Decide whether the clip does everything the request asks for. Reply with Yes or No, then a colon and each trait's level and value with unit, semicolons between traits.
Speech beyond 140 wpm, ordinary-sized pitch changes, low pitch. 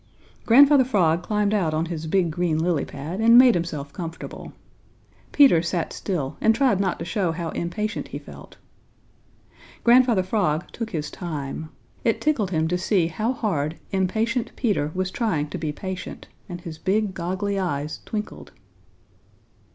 No: average, 155 wpm; average, 4.9 semitones; medium, 185 Hz